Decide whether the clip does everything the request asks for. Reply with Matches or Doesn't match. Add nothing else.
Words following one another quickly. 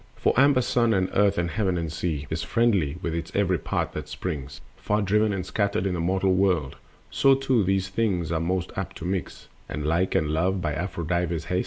Matches